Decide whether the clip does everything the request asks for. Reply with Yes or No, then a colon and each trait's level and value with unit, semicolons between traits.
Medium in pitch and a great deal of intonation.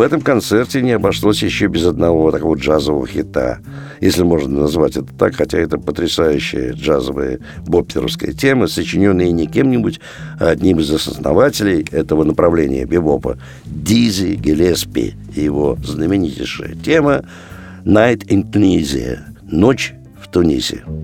No: very low, 90 Hz; wide, 5.8 semitones